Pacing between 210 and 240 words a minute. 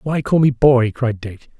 Yes: fast, 225 wpm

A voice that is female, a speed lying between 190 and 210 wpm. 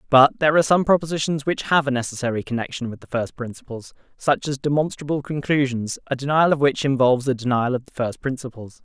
No: male; average, 195 wpm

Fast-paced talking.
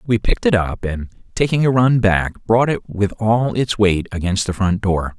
Yes: fast, 220 wpm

